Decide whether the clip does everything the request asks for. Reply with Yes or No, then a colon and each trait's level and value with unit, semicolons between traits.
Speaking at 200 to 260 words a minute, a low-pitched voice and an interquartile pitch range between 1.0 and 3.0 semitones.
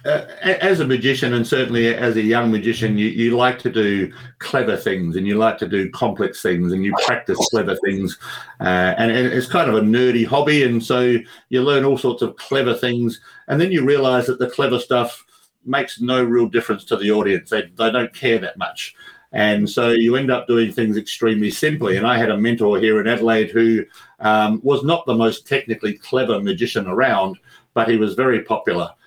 Yes: fast, 205 wpm; low, 115 Hz; average, 2.7 semitones